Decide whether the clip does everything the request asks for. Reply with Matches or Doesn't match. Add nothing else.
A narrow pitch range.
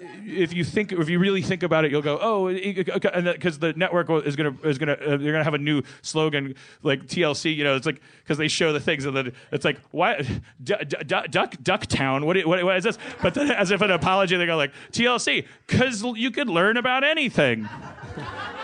Doesn't match